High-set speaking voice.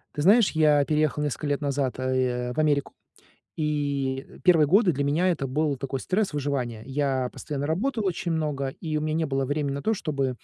No: medium, 145 Hz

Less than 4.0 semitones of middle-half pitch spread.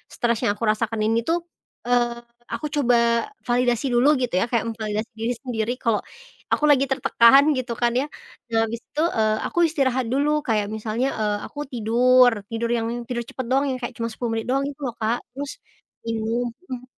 Yes: narrow, 2.4 semitones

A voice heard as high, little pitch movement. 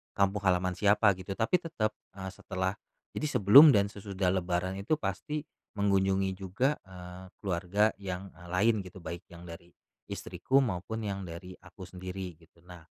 No: very low, 95 Hz; narrow, 2.2 semitones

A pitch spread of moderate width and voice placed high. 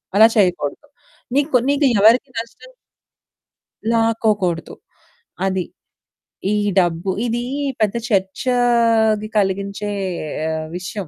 Yes: average, 3.6 semitones; high, 215 Hz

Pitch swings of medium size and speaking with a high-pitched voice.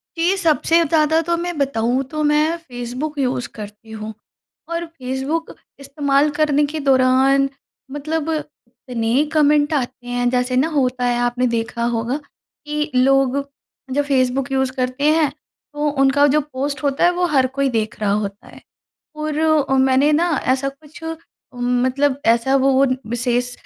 Yes: average, 3.2 semitones; very high, 270 Hz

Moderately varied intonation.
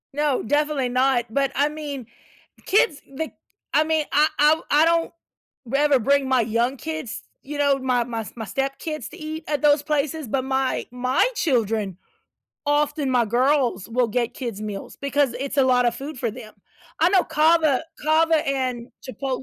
Yes: average, 3.3 semitones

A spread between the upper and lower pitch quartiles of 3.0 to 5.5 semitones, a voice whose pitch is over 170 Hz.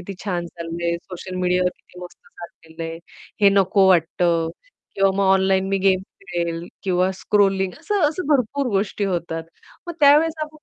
No: narrow, 2.6 semitones; high, 190 Hz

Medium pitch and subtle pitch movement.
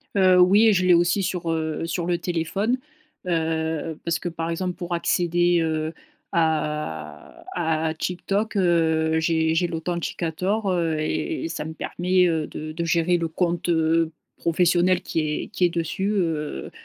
Yes: medium, 170 Hz; narrow, 2.0 semitones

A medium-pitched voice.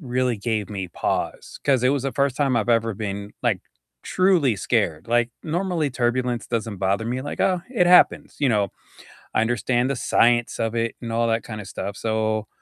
No: low, 120 Hz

